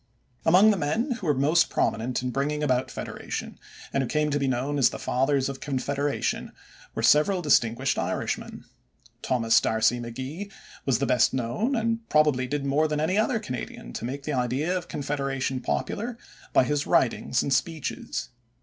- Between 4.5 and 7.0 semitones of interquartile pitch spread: No, average, 3.4 semitones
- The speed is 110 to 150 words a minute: No, average, 170 wpm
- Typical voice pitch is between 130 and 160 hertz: Yes, medium, 140 Hz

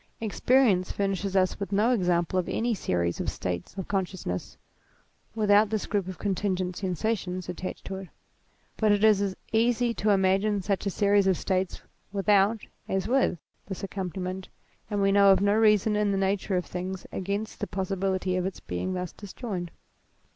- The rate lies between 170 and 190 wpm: Yes, average, 175 wpm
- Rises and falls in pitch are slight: Yes, narrow, 1.9 semitones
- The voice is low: No, high, 195 Hz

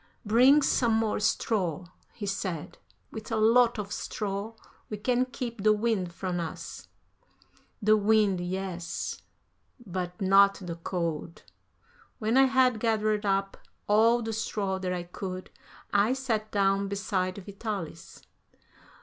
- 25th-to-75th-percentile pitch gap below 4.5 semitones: Yes, average, 3.0 semitones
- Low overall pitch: No, high, 205 Hz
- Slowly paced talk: Yes, slow, 130 wpm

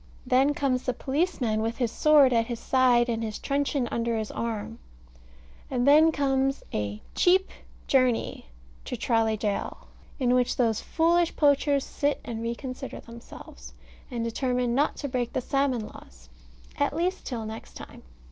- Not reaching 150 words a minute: No, average, 155 wpm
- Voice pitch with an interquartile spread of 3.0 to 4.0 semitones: Yes, average, 3.5 semitones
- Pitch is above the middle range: Yes, very high, 250 Hz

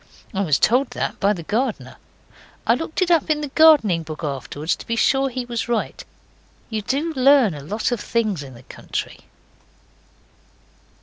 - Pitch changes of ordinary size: No, wide, 7.7 semitones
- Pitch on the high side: Yes, high, 230 Hz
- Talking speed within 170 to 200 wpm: Yes, average, 175 wpm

